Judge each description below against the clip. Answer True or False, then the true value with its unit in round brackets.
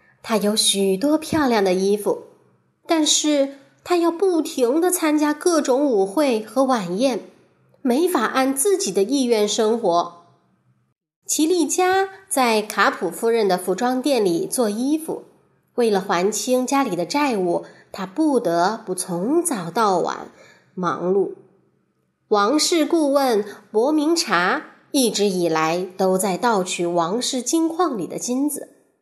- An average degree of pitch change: False (7.8 semitones)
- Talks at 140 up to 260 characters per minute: True (190 characters per minute)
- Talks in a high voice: True (250 Hz)